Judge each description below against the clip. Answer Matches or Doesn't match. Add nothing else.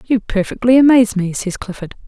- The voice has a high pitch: Matches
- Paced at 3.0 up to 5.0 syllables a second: Doesn't match